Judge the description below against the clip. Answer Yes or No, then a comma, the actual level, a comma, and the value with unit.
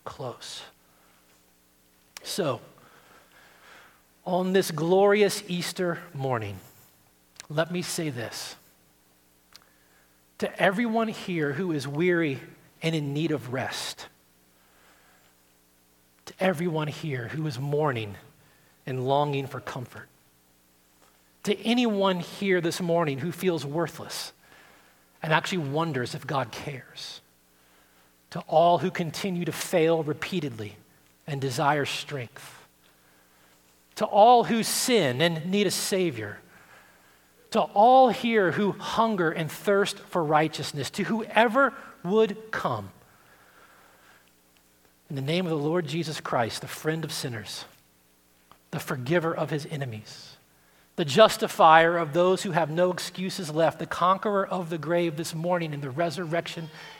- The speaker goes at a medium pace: No, slow, 120 wpm